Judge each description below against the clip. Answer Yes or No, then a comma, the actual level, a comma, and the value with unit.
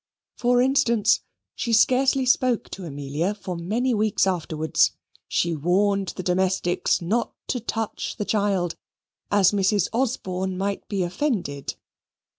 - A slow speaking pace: Yes, slow, 125 wpm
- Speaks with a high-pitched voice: Yes, high, 200 Hz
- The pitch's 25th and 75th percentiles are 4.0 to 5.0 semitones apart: Yes, average, 4.7 semitones